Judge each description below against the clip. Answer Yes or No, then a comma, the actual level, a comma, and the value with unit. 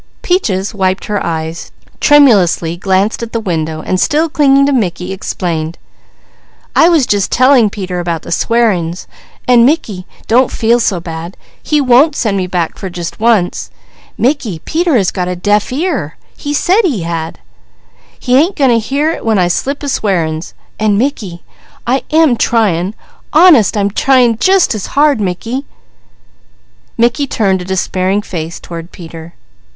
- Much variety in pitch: Yes, wide, 7.1 semitones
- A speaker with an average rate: Yes, average, 155 wpm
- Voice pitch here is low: No, high, 210 Hz